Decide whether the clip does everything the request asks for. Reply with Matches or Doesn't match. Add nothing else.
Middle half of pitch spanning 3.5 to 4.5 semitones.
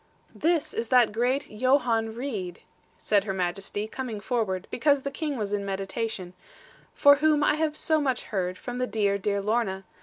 Doesn't match